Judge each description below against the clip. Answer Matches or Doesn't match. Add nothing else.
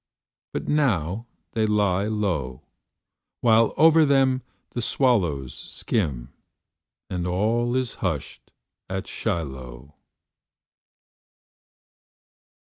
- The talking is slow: Matches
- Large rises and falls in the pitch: Matches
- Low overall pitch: Matches